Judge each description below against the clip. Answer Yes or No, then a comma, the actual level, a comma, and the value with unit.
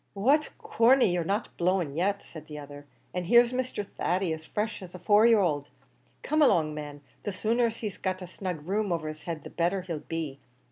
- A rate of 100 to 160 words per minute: No, fast, 205 wpm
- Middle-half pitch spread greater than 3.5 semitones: Yes, average, 5.3 semitones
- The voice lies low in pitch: No, medium, 185 Hz